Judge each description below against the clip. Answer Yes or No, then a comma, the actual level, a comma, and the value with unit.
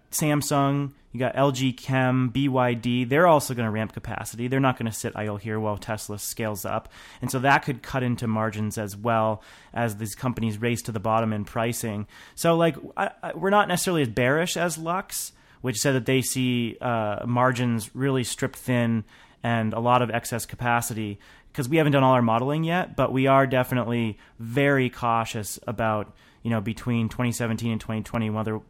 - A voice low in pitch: Yes, low, 120 Hz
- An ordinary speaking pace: Yes, average, 190 wpm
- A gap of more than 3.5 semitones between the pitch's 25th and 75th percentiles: No, average, 3.0 semitones